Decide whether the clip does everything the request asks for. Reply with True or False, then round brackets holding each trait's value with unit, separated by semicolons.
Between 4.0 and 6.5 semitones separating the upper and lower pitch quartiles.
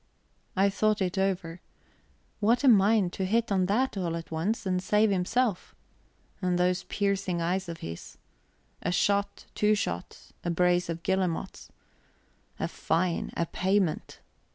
False (2.6 semitones)